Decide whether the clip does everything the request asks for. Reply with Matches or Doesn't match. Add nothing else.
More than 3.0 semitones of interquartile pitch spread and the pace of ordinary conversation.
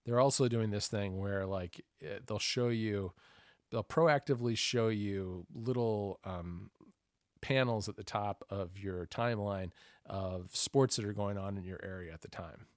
Matches